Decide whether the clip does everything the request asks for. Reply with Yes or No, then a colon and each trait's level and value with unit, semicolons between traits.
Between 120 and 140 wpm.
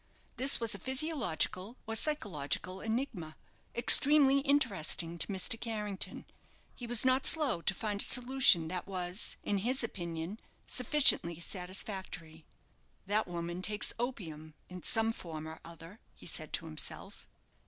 Yes: slow, 135 wpm